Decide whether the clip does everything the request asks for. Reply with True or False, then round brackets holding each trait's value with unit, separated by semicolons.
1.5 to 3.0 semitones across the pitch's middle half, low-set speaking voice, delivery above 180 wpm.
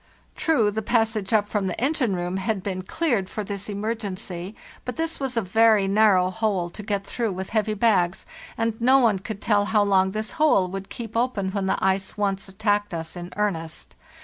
False (2.7 semitones; 205 Hz; 200 wpm)